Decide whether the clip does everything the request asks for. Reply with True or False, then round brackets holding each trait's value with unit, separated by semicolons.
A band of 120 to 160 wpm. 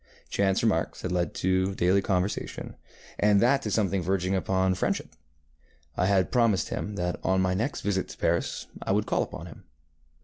False (175 wpm)